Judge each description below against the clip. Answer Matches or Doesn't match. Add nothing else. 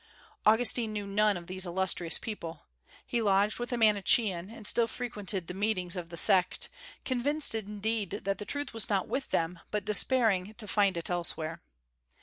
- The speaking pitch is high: Matches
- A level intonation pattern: Doesn't match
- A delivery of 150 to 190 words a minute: Matches